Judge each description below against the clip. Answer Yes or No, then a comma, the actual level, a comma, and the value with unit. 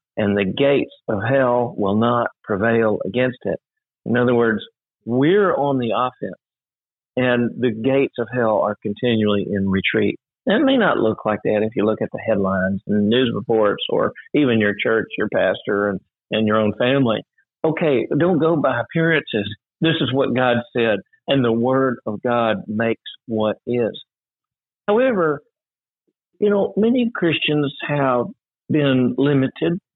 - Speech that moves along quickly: No, average, 160 wpm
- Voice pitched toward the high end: No, low, 120 Hz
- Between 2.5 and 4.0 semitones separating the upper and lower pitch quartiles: No, average, 4.4 semitones